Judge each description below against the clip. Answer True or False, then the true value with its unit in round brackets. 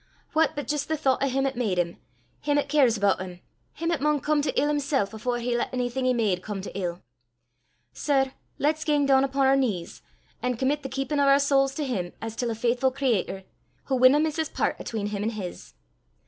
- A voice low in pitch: False (265 Hz)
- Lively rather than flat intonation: False (4.2 semitones)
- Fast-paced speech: True (230 wpm)